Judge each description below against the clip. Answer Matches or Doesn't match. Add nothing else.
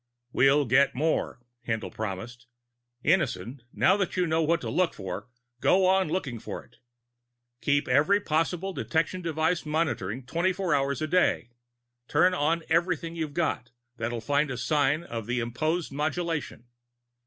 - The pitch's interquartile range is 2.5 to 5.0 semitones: Doesn't match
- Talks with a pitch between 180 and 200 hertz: Doesn't match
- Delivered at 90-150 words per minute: Matches